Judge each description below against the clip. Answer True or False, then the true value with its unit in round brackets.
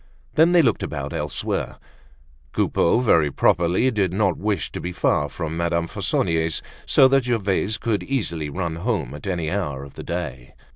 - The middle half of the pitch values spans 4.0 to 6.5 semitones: True (4.8 semitones)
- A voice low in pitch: True (90 Hz)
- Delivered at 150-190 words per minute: True (165 wpm)